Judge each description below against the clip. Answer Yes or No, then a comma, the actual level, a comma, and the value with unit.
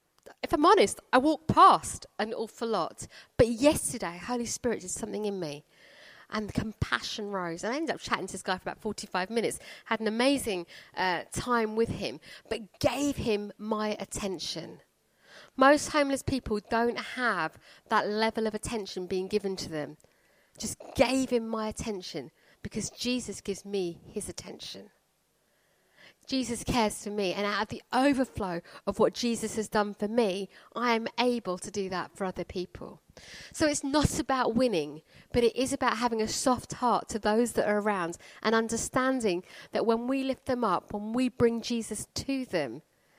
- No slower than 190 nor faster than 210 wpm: No, average, 175 wpm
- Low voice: No, high, 220 Hz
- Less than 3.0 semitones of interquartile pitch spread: No, average, 4.0 semitones